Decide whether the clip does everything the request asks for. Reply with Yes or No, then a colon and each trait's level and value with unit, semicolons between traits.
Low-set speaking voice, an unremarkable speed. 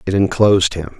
Yes: very low, 95 Hz; average, 180 wpm